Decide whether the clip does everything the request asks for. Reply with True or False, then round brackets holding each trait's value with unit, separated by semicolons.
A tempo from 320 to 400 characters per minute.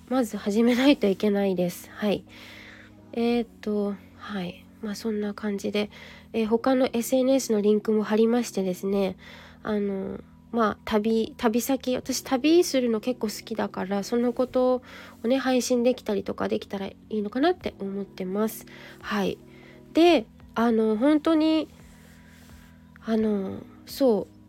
False (260 characters per minute)